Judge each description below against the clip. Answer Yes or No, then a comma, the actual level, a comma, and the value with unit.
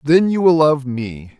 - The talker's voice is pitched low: No, medium, 145 Hz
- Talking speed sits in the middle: No, fast, 215 wpm